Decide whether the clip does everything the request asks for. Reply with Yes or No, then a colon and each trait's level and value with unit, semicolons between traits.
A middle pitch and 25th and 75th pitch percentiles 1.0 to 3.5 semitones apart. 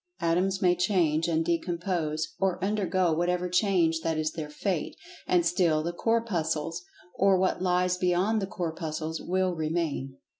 Yes: medium, 175 Hz; narrow, 2.5 semitones